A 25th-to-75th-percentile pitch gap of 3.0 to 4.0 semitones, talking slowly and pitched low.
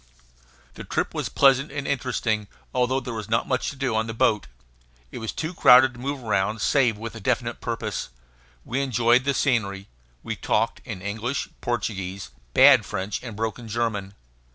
No: average, 3.5 semitones; average, 175 wpm; low, 115 Hz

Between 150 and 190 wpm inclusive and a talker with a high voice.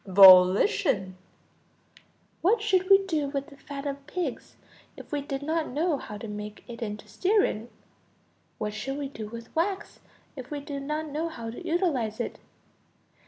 Yes: average, 165 wpm; very high, 280 Hz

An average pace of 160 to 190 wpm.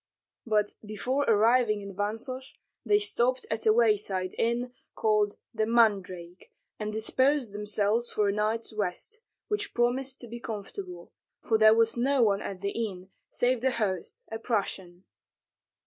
No: average, 150 wpm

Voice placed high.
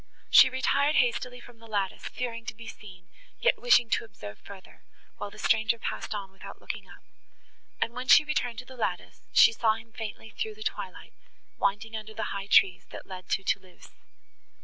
Yes: high, 225 Hz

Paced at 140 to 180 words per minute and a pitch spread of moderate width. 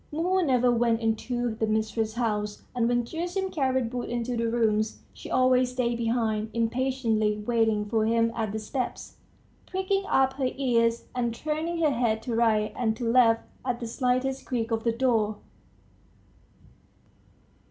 No: average, 155 wpm; narrow, 2.3 semitones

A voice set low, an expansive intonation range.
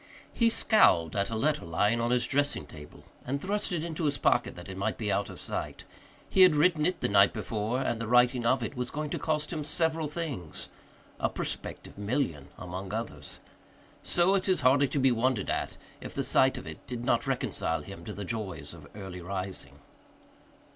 Yes: low, 125 Hz; wide, 7.0 semitones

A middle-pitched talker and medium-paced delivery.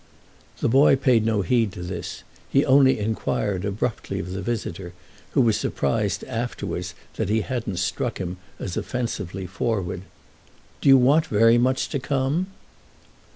No: low, 115 Hz; average, 150 wpm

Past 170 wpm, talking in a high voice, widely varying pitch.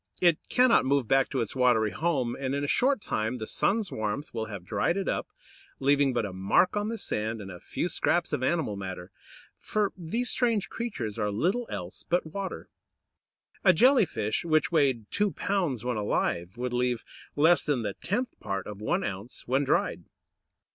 No: average, 190 wpm; low, 130 Hz; wide, 8.9 semitones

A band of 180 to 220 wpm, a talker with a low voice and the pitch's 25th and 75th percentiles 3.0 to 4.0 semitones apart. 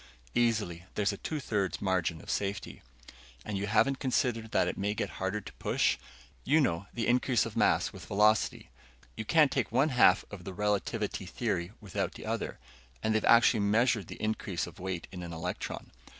Yes: average, 185 wpm; low, 105 Hz; average, 3.6 semitones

